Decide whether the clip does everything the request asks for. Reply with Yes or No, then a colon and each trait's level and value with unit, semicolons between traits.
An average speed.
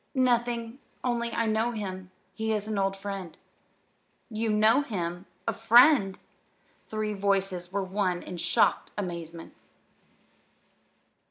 No: slow, 120 wpm